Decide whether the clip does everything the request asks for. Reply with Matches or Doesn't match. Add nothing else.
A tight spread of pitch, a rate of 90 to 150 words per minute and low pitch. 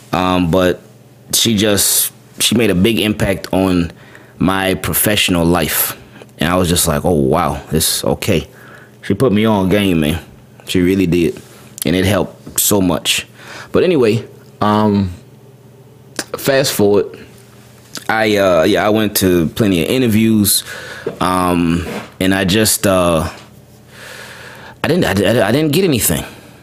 Doesn't match